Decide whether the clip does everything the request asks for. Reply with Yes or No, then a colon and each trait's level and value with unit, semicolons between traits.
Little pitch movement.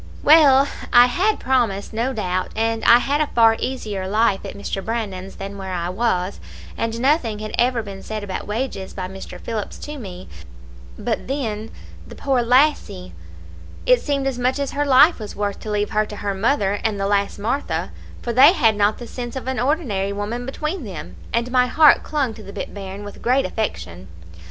No: average, 4.6 semitones